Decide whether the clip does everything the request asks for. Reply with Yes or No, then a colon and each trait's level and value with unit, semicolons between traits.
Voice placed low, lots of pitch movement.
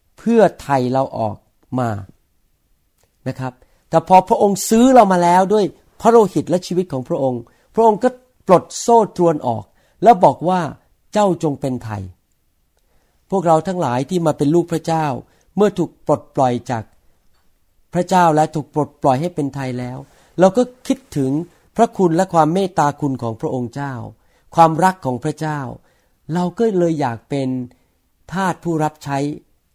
No: medium, 150 Hz; wide, 6.3 semitones